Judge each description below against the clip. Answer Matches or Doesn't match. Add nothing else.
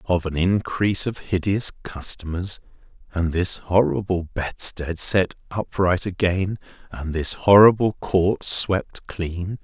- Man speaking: Matches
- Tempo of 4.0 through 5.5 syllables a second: Doesn't match